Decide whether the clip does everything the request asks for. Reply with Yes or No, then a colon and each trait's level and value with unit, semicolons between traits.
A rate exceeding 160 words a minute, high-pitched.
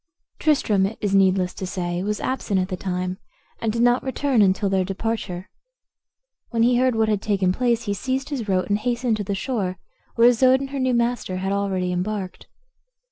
Yes: average, 195 wpm; high, 210 Hz